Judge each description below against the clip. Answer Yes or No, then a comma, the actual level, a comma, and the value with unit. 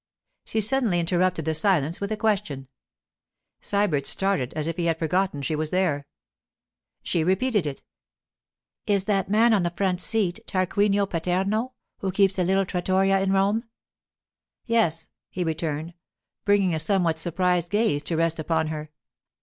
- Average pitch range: Yes, average, 3.5 semitones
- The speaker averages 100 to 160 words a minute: Yes, average, 150 wpm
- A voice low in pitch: No, medium, 185 Hz